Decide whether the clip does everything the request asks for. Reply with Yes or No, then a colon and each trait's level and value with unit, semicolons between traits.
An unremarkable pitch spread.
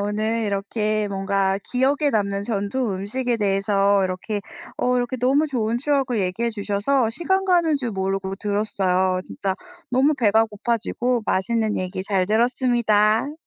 Yes: average, 3.9 semitones